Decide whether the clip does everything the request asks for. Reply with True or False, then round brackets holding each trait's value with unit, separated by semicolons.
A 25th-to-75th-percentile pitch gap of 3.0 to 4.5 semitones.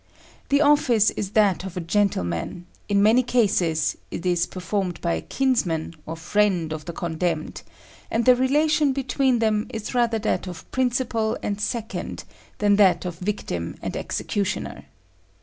False (5.4 semitones)